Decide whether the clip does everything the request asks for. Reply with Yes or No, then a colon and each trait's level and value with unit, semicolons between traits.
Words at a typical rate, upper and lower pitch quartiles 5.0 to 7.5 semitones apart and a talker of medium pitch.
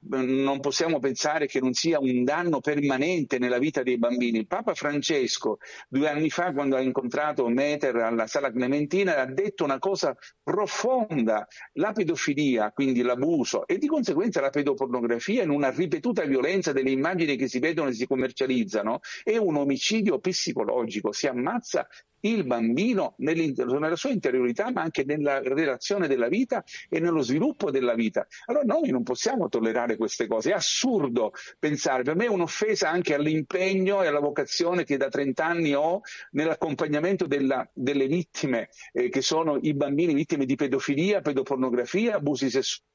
Yes: average, 155 wpm; wide, 5.5 semitones; medium, 145 Hz